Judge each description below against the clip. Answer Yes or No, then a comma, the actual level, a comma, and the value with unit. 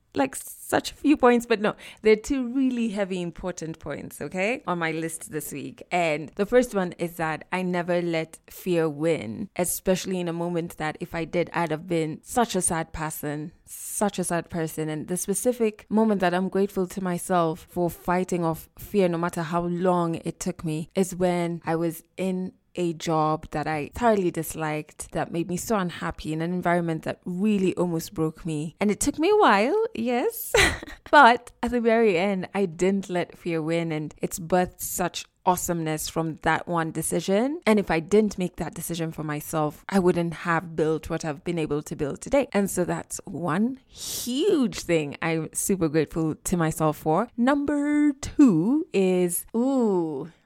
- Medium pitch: Yes, medium, 175 Hz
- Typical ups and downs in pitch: Yes, average, 3.6 semitones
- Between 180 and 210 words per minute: Yes, average, 185 wpm